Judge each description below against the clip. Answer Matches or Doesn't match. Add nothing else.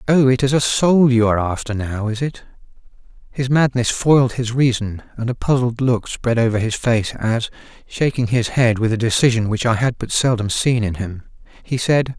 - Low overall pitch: Matches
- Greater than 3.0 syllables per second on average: Matches